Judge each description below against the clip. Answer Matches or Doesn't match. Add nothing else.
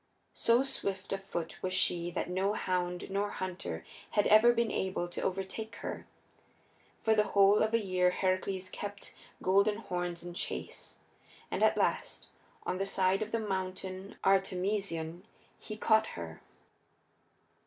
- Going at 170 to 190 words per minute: Doesn't match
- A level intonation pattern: Matches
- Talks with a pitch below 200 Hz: Matches